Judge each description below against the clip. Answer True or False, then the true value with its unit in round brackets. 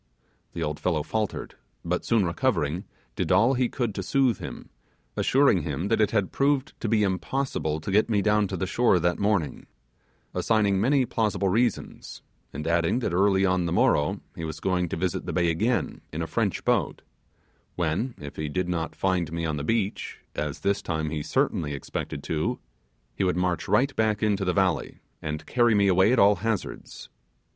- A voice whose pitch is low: True (95 Hz)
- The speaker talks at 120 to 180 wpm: False (190 wpm)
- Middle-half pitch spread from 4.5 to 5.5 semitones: True (4.8 semitones)